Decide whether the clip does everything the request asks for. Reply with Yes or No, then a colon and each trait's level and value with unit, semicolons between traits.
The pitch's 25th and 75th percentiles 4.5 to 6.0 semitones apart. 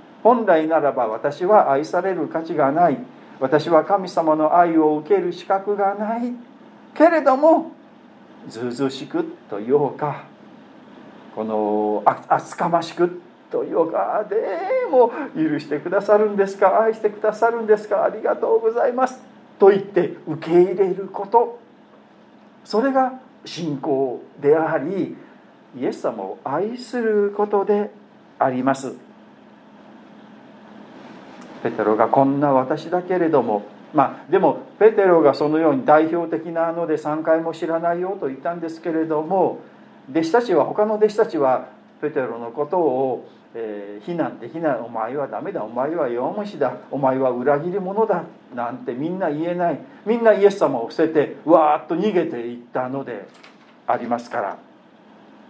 No: wide, 6.6 semitones